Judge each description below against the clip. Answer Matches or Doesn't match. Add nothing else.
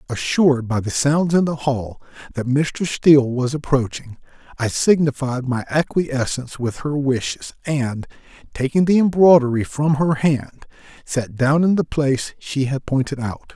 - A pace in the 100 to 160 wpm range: Matches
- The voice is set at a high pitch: Doesn't match